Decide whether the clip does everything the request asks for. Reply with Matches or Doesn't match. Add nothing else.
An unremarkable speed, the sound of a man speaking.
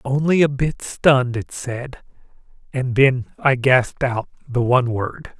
Matches